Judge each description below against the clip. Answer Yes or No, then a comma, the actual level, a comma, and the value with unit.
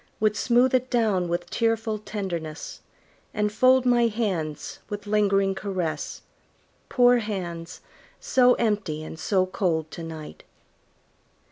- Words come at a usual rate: No, slow, 120 wpm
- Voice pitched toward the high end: Yes, high, 205 Hz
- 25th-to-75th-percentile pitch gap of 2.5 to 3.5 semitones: No, average, 4.8 semitones